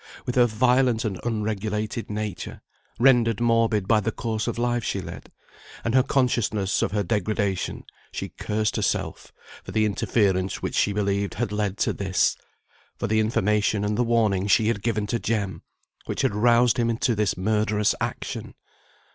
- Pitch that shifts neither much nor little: No, narrow, 2.2 semitones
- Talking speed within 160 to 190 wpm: Yes, average, 165 wpm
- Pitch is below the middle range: Yes, low, 110 Hz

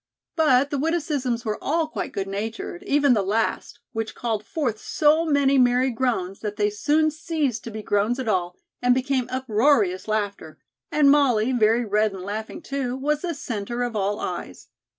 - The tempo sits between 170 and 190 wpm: Yes, average, 175 wpm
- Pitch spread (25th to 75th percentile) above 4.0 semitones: Yes, average, 5.0 semitones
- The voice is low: No, high, 245 Hz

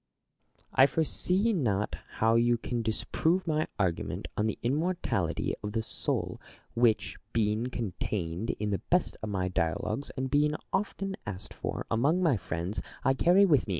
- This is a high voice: No, low, 120 Hz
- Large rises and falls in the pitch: Yes, wide, 7.0 semitones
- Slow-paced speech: No, average, 160 wpm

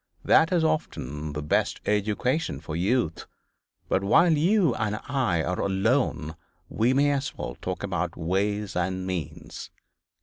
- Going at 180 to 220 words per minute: No, average, 140 wpm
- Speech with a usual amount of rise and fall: No, wide, 7.5 semitones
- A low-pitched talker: Yes, low, 100 Hz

